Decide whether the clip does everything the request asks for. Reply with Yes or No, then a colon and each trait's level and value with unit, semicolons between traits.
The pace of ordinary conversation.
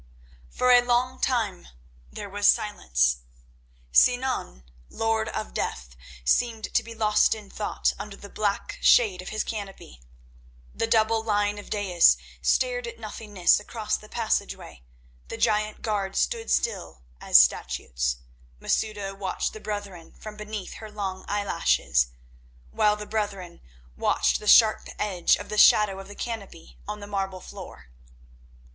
Yes: average, 145 wpm